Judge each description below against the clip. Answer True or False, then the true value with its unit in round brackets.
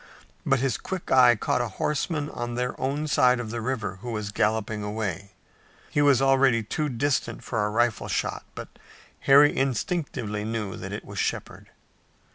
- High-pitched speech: False (120 Hz)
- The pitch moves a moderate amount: True (4.0 semitones)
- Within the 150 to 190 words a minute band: True (170 wpm)